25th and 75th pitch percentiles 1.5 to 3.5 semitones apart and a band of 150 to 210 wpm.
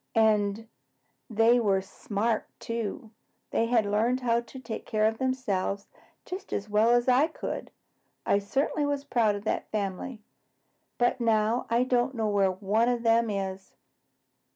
Yes: average, 2.9 semitones; average, 155 wpm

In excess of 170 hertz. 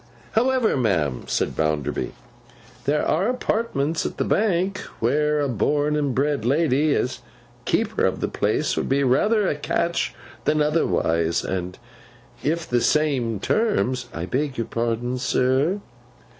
No: medium, 140 Hz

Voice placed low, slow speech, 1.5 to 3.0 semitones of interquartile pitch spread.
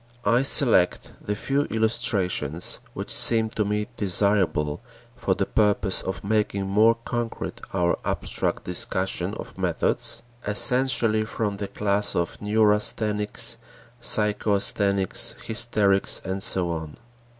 Yes: low, 105 Hz; slow, 115 wpm; narrow, 2.5 semitones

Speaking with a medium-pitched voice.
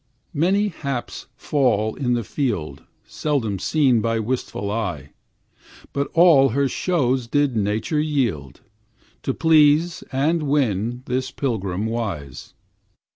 No: low, 125 Hz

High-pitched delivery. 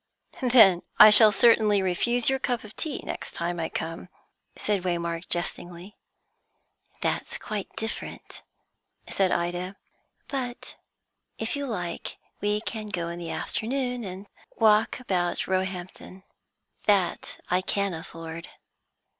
Yes: high, 195 Hz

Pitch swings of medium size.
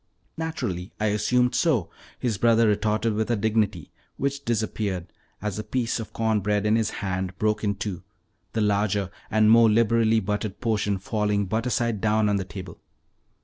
No: narrow, 2.0 semitones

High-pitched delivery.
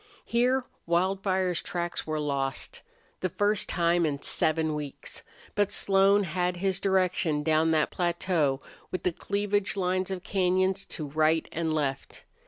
No: medium, 180 Hz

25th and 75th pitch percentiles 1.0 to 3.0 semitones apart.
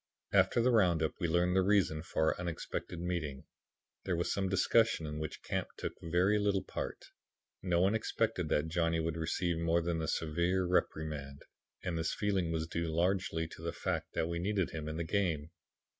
Yes: average, 2.7 semitones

